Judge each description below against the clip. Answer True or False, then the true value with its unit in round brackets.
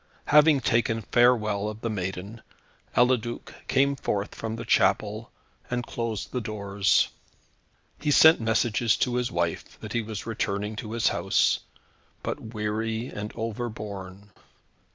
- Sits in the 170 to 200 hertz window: False (110 Hz)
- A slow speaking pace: True (130 wpm)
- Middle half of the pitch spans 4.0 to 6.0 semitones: False (2.4 semitones)